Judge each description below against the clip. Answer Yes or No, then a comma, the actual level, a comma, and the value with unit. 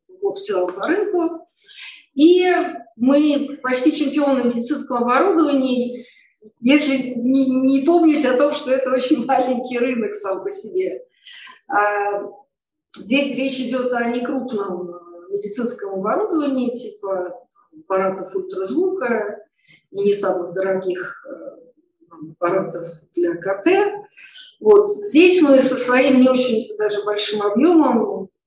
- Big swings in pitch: Yes, wide, 7.1 semitones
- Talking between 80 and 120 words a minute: Yes, slow, 110 wpm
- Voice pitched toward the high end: Yes, very high, 255 Hz